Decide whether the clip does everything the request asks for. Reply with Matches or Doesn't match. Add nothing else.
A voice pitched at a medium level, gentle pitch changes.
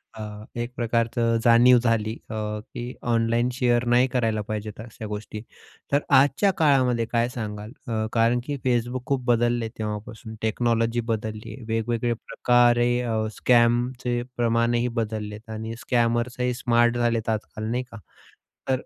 Doesn't match